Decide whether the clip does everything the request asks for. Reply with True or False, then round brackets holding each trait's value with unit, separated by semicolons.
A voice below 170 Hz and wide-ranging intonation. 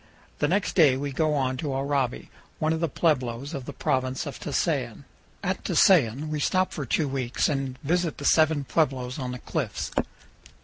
False (140 Hz; 3.3 semitones)